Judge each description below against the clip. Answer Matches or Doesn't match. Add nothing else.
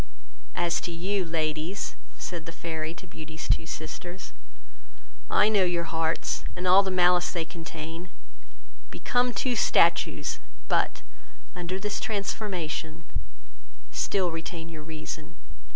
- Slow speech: Matches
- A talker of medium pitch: Matches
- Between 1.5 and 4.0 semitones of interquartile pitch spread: Matches